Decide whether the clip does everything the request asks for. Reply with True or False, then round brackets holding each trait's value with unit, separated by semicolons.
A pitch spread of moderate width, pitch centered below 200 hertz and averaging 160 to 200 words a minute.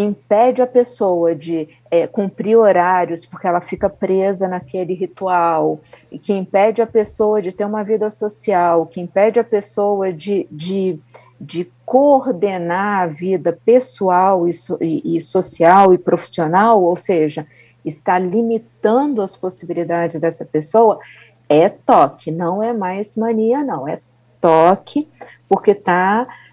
False (3.8 semitones; 190 Hz; 135 wpm)